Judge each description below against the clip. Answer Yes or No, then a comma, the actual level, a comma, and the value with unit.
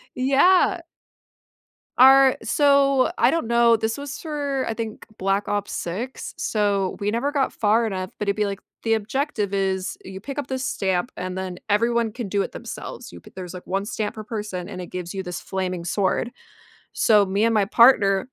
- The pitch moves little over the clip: No, average, 4.9 semitones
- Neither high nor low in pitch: No, high, 210 Hz